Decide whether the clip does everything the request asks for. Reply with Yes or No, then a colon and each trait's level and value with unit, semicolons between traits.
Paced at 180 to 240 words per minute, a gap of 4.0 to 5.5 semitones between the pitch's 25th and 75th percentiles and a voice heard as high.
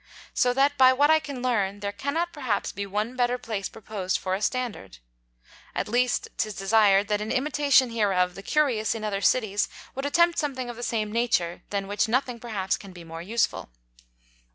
Yes: average, 190 wpm; average, 4.3 semitones; high, 225 Hz